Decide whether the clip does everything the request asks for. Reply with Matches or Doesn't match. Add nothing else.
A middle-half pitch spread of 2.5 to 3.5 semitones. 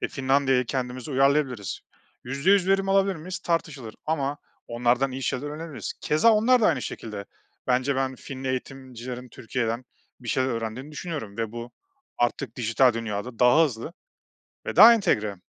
Doesn't match